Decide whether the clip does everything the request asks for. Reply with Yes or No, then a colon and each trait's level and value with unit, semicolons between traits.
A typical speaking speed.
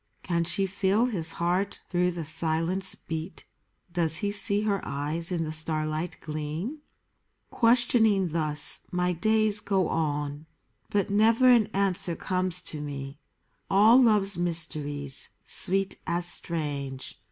No: slow, 130 wpm